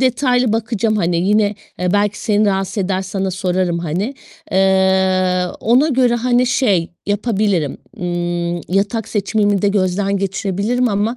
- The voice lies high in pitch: Yes, high, 200 Hz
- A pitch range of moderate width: Yes, average, 3.0 semitones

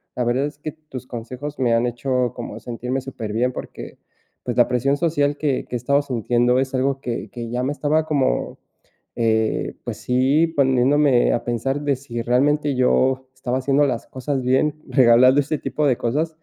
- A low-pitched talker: Yes, low, 130 Hz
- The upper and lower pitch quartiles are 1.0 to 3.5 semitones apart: Yes, average, 2.8 semitones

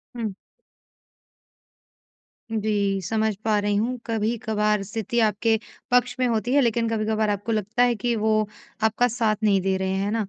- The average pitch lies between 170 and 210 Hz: No, high, 220 Hz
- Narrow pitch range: Yes, narrow, 1.8 semitones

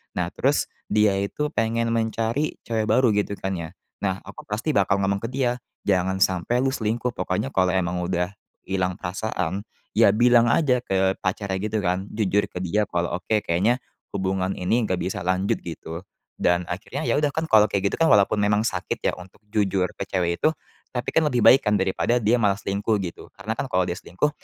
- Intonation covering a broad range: No, average, 3.7 semitones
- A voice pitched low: Yes, low, 100 Hz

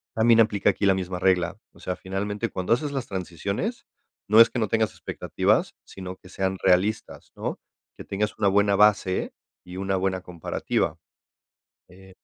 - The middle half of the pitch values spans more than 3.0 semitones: No, narrow, 2.4 semitones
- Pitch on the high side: No, very low, 95 Hz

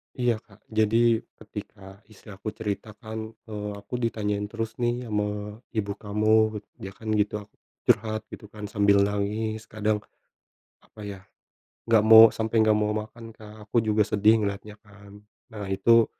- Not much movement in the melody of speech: Yes, narrow, 1.3 semitones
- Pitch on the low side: Yes, low, 105 Hz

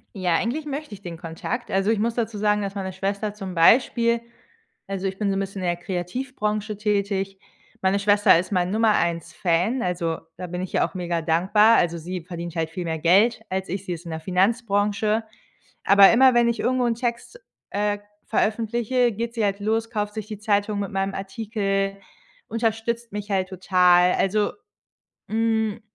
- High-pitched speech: Yes, high, 200 Hz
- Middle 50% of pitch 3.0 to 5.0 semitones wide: Yes, average, 3.3 semitones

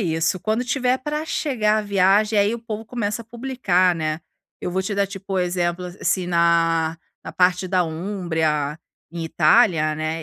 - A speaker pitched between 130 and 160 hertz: No, medium, 185 Hz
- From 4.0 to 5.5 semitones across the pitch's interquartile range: Yes, average, 4.5 semitones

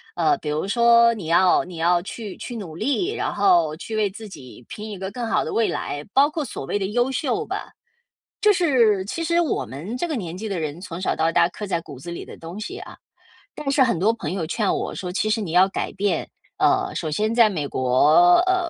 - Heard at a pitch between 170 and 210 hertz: Yes, high, 205 Hz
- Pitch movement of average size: No, wide, 6.1 semitones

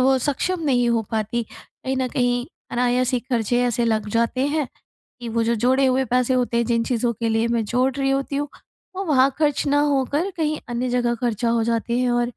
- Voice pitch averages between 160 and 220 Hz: No, high, 245 Hz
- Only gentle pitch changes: Yes, narrow, 2.2 semitones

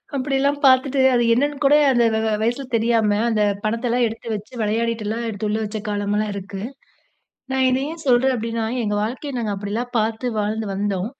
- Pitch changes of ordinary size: Yes, average, 3.3 semitones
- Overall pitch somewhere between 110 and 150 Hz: No, high, 230 Hz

